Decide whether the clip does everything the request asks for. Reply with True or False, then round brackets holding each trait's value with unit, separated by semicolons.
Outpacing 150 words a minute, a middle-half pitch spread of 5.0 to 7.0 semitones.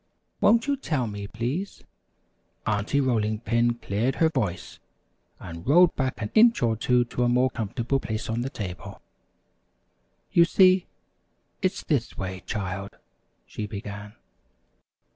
False (135 wpm; 5.3 semitones)